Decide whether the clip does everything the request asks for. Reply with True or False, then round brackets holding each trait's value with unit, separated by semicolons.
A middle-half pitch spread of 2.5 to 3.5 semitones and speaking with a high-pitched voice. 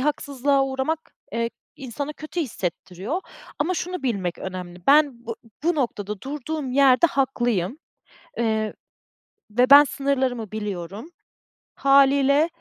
False (4.7 semitones; 265 Hz)